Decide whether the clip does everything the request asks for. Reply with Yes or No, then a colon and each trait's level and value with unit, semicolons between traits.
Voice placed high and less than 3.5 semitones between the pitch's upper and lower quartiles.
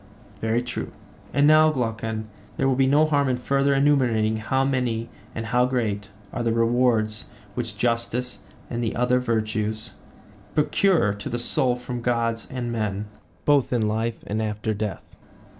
No: low, 120 Hz; average, 2.7 semitones